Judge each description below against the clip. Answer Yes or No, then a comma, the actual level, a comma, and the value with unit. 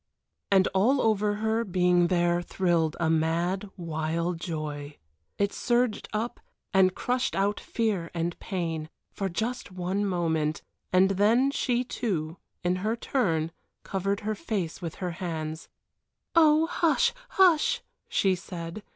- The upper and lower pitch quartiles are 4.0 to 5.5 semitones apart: Yes, average, 4.6 semitones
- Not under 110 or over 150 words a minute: Yes, slow, 135 wpm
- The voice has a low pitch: No, medium, 185 Hz